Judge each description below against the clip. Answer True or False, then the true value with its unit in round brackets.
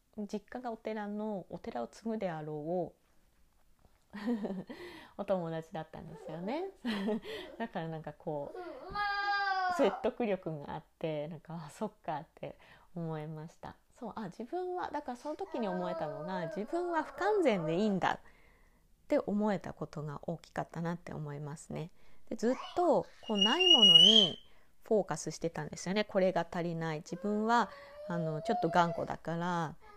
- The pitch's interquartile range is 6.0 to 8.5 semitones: True (6.6 semitones)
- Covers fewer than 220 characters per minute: False (305 characters per minute)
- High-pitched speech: True (200 Hz)